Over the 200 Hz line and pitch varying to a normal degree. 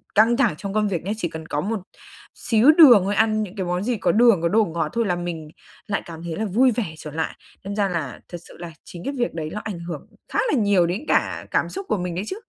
No: high, 195 Hz; average, 4.5 semitones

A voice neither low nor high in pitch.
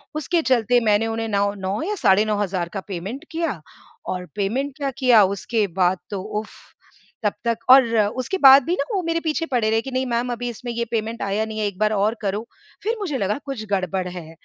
No: high, 225 Hz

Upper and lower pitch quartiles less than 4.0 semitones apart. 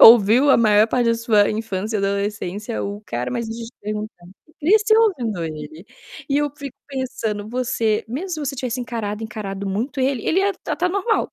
No: average, 4.3 semitones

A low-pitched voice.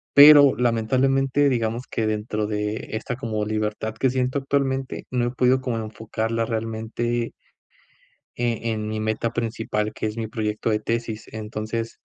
Yes: low, 115 Hz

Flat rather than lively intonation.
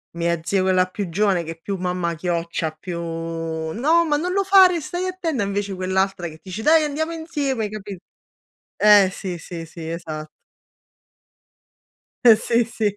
No: wide, 7.9 semitones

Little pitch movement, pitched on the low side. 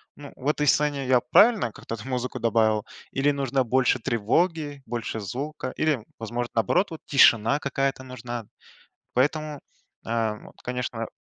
No: average, 3.8 semitones; low, 130 Hz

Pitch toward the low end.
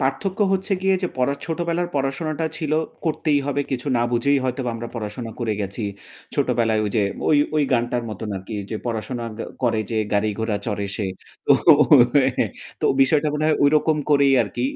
Yes: low, 130 Hz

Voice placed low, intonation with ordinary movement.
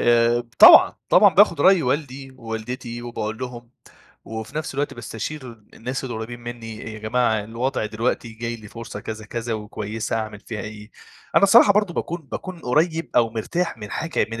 Yes: low, 120 Hz; average, 3.4 semitones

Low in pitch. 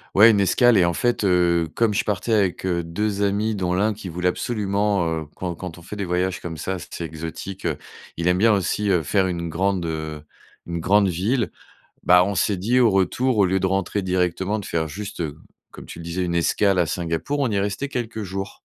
Yes: very low, 95 Hz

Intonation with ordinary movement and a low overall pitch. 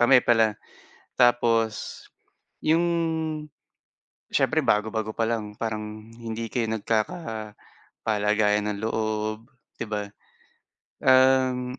Yes: average, 3.1 semitones; low, 115 Hz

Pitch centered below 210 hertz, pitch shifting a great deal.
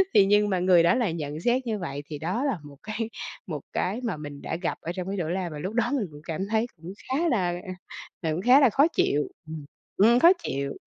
Yes: medium, 185 Hz; wide, 6.5 semitones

